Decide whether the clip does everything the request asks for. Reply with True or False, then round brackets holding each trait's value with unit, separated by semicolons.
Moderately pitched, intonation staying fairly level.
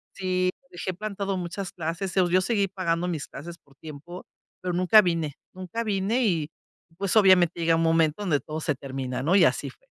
False (180 Hz; 3.0 semitones)